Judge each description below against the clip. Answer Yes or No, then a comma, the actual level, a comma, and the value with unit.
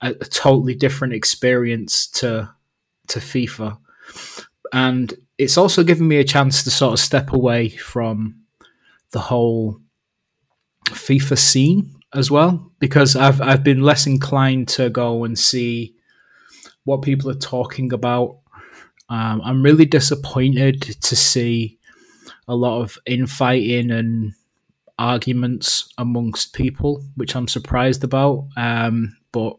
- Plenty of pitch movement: No, narrow, 2.6 semitones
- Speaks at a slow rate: Yes, slow, 125 wpm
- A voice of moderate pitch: No, low, 125 Hz